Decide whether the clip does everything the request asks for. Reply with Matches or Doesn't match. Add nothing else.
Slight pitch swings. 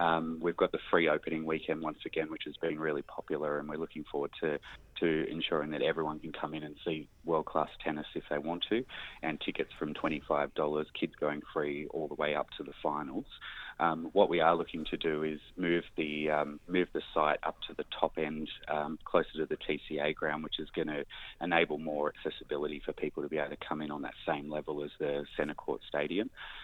Matches